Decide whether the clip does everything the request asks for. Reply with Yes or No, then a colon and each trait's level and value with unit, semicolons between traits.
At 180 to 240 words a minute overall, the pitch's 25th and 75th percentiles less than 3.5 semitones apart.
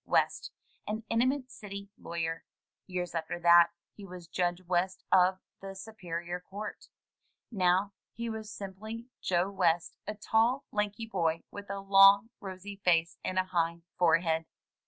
No: average, 140 wpm; average, 3.0 semitones